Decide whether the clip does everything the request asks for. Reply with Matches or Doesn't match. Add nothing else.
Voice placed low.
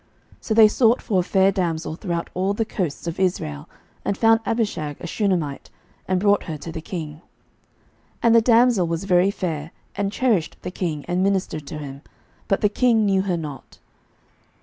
Doesn't match